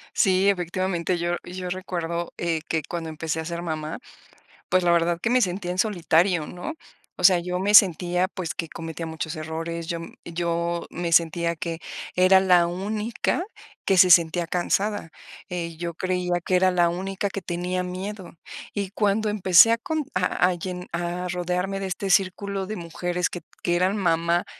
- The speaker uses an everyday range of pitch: No, narrow, 1.8 semitones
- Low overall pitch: No, medium, 180 Hz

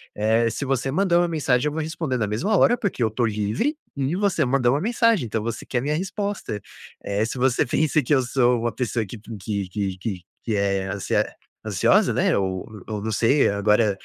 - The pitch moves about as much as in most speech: No, wide, 6.1 semitones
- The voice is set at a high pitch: No, low, 120 Hz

